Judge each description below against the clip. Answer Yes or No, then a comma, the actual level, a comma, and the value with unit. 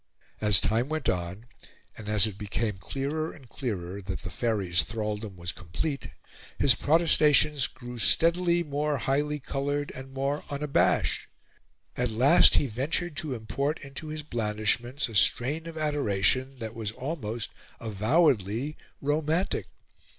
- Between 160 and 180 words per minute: No, slow, 135 wpm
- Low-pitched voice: Yes, low, 130 Hz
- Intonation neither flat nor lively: No, wide, 5.8 semitones